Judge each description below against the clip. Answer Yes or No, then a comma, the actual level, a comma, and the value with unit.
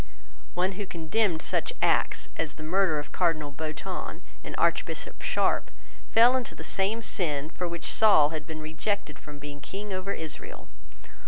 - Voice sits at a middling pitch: Yes, medium, 165 Hz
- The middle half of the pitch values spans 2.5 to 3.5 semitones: No, average, 4.3 semitones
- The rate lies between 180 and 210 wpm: No, average, 160 wpm